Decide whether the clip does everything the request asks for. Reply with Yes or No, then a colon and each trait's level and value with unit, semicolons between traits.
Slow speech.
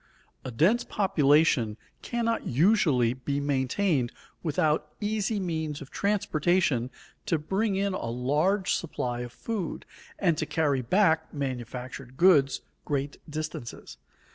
Yes: slow, 115 wpm